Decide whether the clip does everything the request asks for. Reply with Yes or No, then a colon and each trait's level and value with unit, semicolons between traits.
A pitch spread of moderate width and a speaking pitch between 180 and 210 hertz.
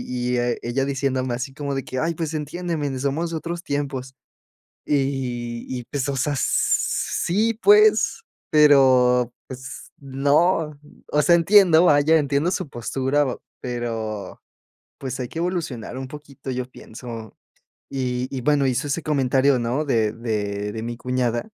No: average, 3.3 semitones; low, 135 Hz